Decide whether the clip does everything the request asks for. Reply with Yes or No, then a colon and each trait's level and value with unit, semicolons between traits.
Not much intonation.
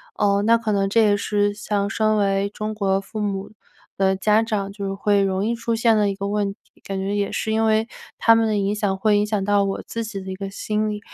Yes: narrow, 1.6 semitones